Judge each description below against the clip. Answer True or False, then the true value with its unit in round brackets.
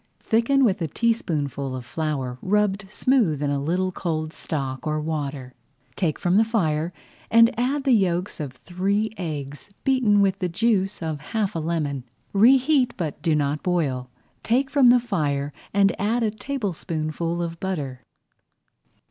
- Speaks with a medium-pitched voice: True (175 Hz)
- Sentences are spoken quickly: False (155 wpm)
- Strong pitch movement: True (6.4 semitones)